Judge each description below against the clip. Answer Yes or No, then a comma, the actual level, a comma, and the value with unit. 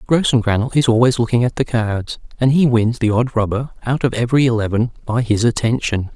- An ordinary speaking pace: Yes, average, 195 wpm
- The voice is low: Yes, low, 120 Hz